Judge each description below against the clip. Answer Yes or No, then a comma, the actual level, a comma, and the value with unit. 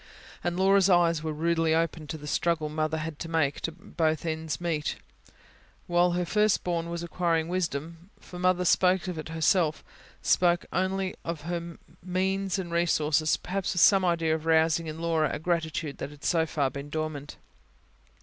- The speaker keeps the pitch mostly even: Yes, narrow, 2.1 semitones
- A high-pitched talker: No, medium, 165 Hz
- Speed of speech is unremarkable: Yes, average, 175 wpm